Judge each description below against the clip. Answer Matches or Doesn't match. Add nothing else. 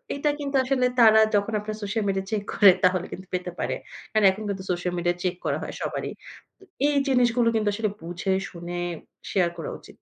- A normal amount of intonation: Matches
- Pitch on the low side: Doesn't match